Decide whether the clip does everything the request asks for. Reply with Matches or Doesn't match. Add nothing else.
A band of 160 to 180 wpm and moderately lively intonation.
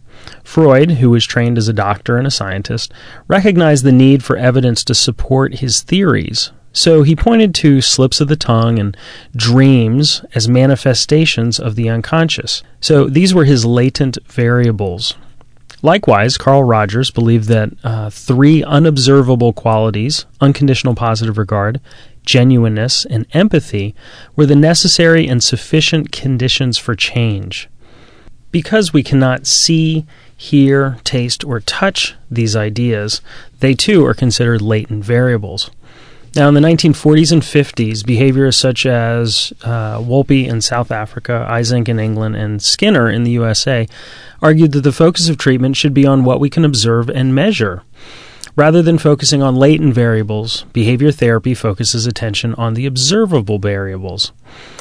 Doesn't match